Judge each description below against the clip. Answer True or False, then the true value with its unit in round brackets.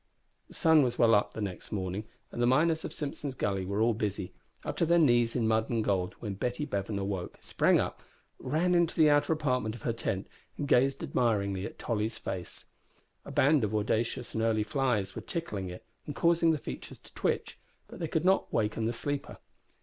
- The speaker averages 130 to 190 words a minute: False (205 wpm)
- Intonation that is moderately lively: False (6.1 semitones)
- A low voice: True (115 Hz)